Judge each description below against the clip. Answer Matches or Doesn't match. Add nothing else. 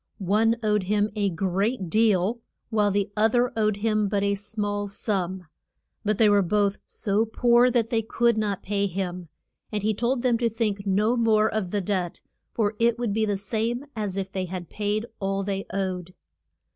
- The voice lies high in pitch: Matches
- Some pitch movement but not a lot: Doesn't match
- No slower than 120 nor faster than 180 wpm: Doesn't match